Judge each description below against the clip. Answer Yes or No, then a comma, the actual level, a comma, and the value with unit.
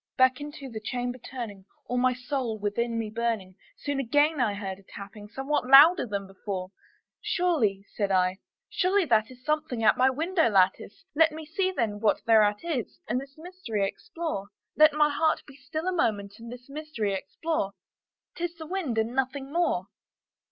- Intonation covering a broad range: Yes, wide, 6.5 semitones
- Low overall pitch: No, very high, 250 Hz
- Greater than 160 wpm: Yes, average, 175 wpm